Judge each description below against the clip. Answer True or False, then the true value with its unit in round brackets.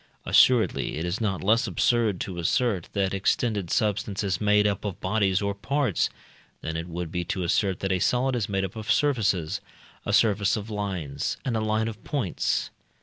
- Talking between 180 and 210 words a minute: True (190 wpm)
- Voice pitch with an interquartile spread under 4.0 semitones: True (3.1 semitones)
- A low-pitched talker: True (100 Hz)